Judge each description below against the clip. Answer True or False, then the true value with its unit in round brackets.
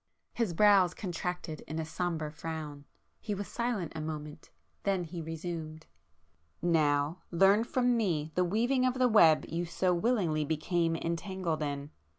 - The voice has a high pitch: False (170 Hz)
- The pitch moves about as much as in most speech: True (4.1 semitones)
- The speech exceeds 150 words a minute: False (140 wpm)